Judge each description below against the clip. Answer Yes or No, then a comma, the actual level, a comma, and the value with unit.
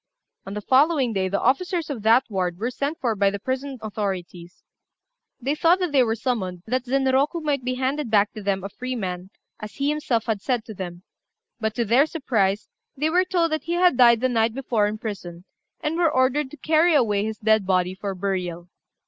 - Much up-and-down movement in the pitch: Yes, wide, 5.7 semitones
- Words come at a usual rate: No, fast, 210 wpm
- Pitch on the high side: Yes, high, 235 Hz